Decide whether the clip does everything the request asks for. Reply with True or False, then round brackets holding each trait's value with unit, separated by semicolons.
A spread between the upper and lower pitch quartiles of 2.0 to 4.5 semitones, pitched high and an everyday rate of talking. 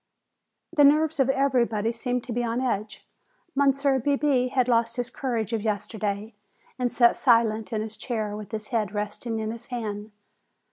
True (3.0 semitones; 235 Hz; 170 wpm)